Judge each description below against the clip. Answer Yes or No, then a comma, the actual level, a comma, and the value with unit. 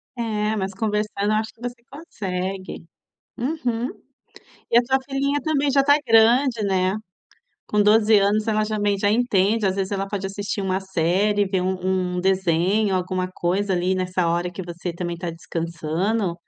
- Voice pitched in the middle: No, high, 200 Hz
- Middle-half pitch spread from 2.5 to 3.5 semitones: Yes, average, 3.2 semitones